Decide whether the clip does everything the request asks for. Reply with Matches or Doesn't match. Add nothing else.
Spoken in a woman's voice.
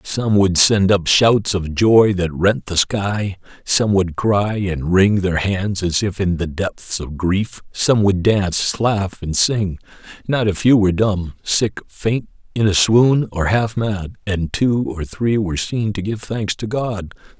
Doesn't match